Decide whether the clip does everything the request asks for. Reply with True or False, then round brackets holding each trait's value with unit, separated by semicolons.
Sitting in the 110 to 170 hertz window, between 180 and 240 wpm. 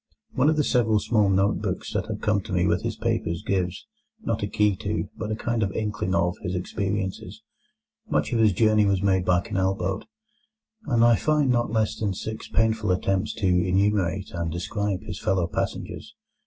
False (100 Hz; 190 wpm)